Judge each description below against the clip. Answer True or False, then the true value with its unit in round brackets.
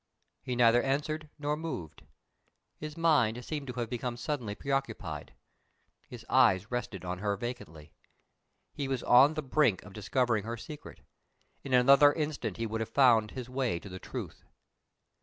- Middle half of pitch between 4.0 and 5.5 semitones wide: True (4.6 semitones)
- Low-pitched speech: True (125 Hz)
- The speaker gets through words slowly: False (160 wpm)